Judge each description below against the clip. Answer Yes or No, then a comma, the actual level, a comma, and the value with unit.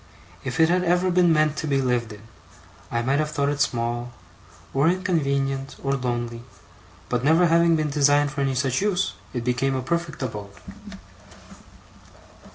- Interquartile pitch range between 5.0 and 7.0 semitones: No, average, 4.5 semitones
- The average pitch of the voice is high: No, medium, 140 Hz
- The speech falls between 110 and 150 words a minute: No, average, 165 wpm